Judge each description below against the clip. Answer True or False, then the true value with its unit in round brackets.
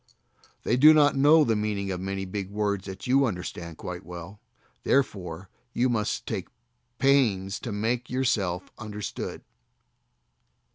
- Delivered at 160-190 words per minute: False (135 wpm)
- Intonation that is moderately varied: True (4.8 semitones)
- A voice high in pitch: False (105 Hz)